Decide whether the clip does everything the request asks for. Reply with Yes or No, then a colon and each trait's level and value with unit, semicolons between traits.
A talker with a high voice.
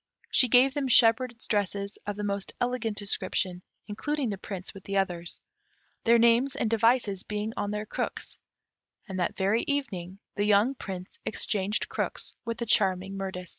Yes: high, 210 Hz